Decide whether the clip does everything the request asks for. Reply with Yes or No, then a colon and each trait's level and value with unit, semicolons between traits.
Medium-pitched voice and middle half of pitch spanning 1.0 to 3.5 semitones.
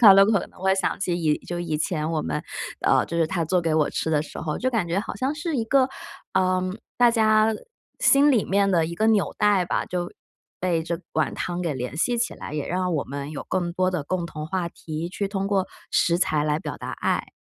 No: medium, 180 Hz; average, 3.9 semitones